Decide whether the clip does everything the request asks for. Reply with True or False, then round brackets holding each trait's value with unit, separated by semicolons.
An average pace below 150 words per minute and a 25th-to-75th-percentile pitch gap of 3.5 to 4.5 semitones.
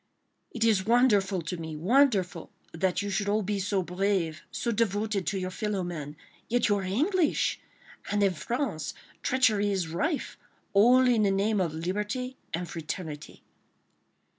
True (140 wpm; 3.9 semitones)